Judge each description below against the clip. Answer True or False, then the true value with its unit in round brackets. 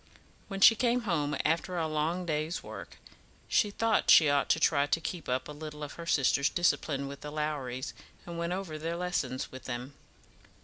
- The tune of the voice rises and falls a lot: False (3.5 semitones)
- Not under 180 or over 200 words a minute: True (190 wpm)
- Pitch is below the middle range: False (155 Hz)